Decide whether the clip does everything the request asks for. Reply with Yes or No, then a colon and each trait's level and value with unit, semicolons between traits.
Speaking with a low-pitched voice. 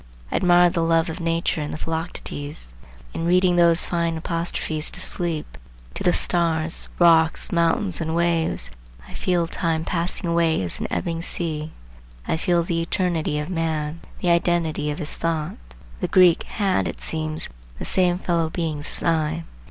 No: medium, 165 Hz